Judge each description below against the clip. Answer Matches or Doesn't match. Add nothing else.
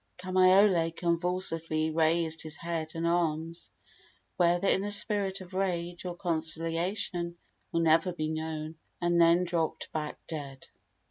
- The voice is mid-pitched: Matches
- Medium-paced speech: Doesn't match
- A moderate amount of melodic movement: Doesn't match